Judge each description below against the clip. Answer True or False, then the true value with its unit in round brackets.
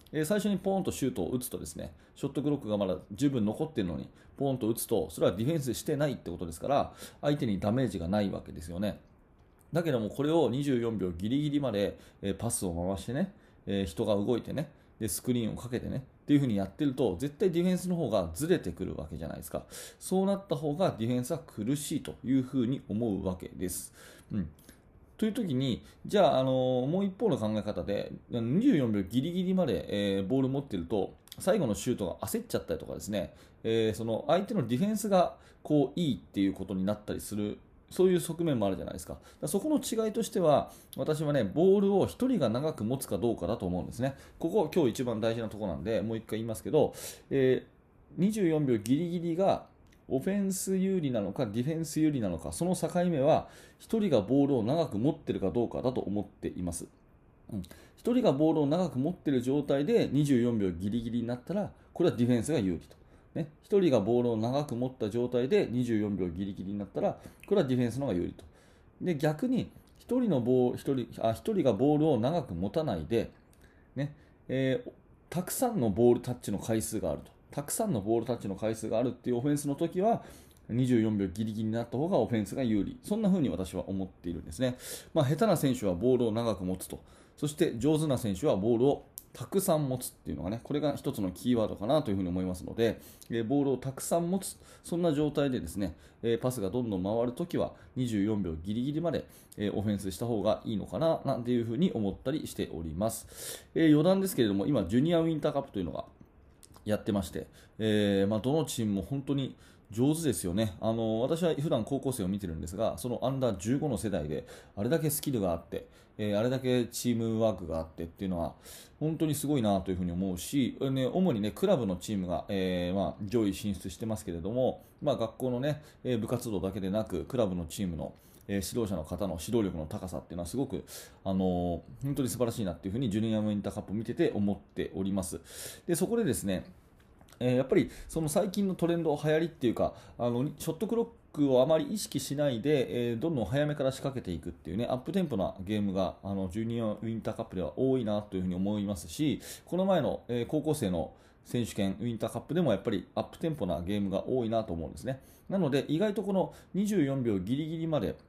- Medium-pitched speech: False (120 Hz)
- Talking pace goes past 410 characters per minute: True (435 characters per minute)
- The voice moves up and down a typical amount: False (7.2 semitones)